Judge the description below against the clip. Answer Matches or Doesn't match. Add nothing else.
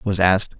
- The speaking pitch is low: Matches